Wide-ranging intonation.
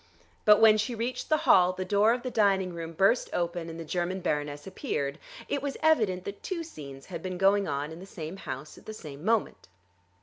No: average, 4.9 semitones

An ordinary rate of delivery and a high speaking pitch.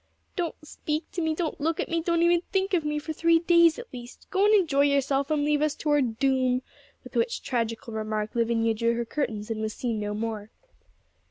No: fast, 220 wpm; very high, 285 Hz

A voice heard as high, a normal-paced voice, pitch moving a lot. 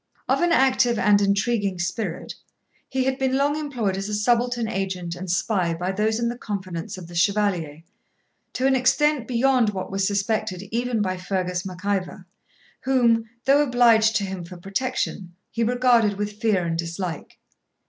No: high, 210 Hz; average, 170 wpm; average, 4.8 semitones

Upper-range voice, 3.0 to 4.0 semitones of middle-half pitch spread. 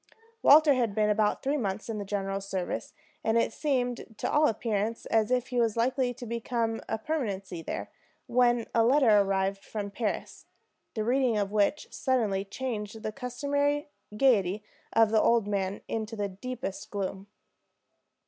Yes: high, 225 Hz; average, 3.6 semitones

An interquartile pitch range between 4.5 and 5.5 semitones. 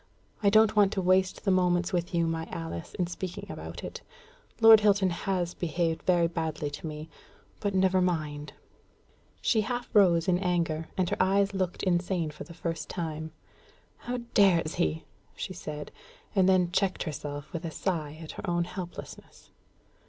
No: average, 2.8 semitones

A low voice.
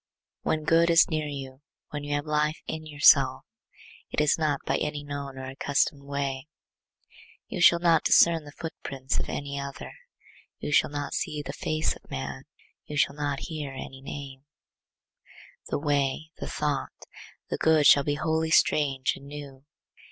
No: medium, 145 Hz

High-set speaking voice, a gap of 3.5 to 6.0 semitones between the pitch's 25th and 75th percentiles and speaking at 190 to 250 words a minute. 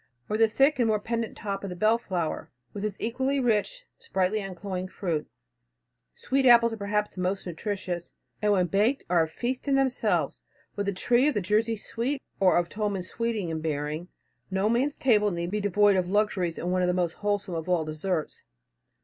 Yes: high, 205 Hz; average, 4.2 semitones; average, 195 wpm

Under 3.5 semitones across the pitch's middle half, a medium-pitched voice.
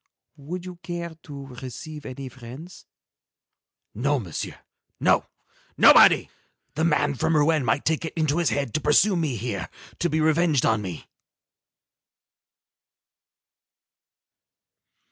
No: average, 4.1 semitones; medium, 150 Hz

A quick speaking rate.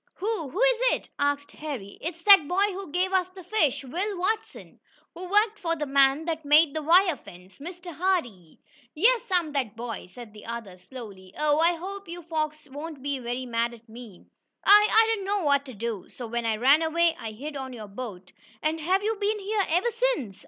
Yes: fast, 210 wpm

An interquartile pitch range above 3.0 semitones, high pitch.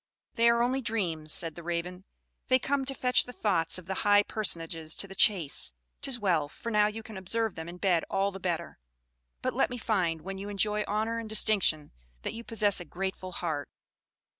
Yes: average, 4.4 semitones; high, 195 Hz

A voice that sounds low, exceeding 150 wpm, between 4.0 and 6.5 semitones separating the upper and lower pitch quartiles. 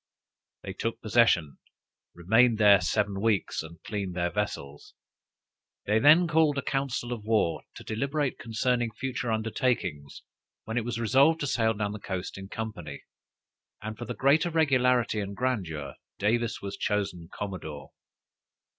No: low, 110 Hz; average, 145 wpm; average, 4.3 semitones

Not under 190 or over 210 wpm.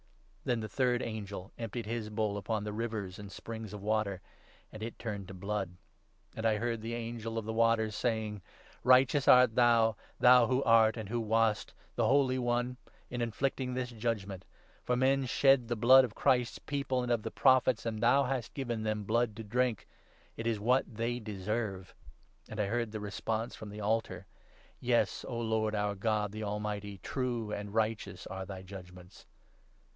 Yes: average, 200 wpm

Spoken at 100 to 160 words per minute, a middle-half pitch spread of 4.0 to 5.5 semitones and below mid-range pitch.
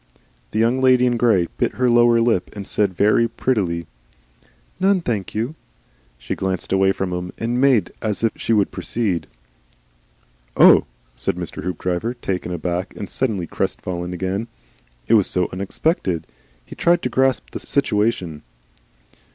Yes: average, 150 wpm; average, 4.8 semitones; low, 105 Hz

